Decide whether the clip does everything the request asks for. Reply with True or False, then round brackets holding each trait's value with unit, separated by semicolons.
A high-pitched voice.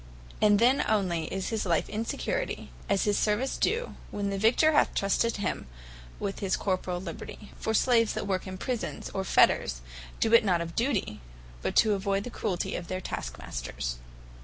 True (200 Hz)